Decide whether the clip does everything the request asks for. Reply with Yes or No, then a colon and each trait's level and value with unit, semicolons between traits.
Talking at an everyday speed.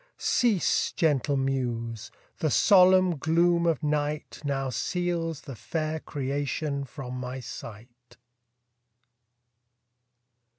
No: slow, 90 wpm